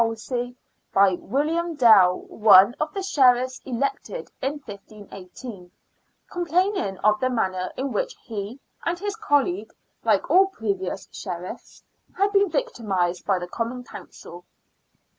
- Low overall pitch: No, high, 245 Hz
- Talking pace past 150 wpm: No, slow, 135 wpm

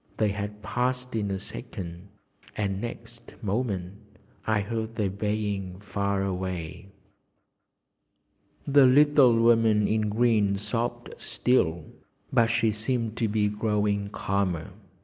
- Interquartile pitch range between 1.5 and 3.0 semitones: Yes, average, 2.7 semitones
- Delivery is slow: Yes, slow, 115 wpm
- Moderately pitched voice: No, low, 105 Hz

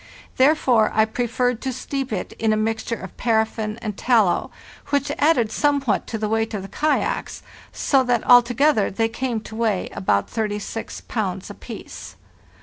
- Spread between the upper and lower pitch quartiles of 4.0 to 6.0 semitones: No, average, 3.0 semitones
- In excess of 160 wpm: No, average, 155 wpm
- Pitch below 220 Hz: No, high, 225 Hz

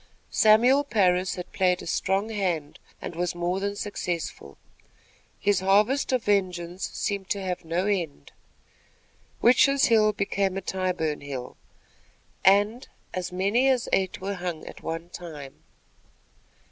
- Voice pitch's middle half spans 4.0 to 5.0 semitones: No, average, 2.9 semitones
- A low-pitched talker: No, high, 190 Hz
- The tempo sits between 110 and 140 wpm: Yes, slow, 135 wpm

